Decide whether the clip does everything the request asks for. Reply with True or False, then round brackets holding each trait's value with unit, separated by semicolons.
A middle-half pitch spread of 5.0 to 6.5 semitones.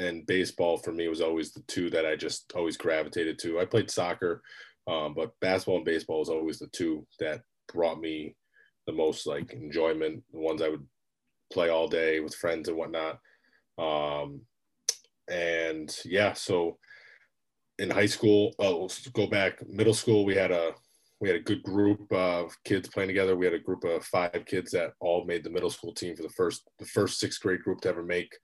True (5.6 semitones)